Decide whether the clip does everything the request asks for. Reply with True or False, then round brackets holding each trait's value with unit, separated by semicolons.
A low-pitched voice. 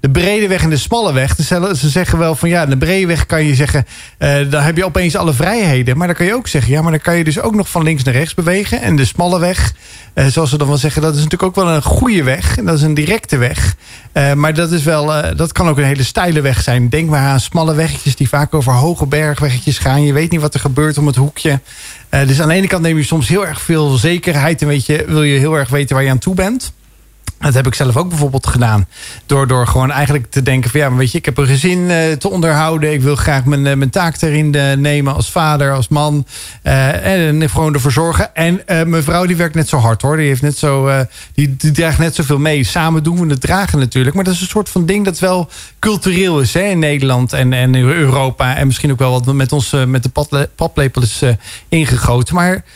False (150 Hz)